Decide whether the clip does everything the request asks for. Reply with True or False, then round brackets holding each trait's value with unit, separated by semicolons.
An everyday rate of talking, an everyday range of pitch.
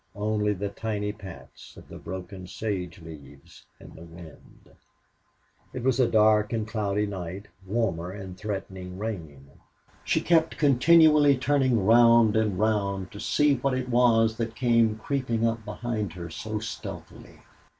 True (145 wpm; 3.7 semitones)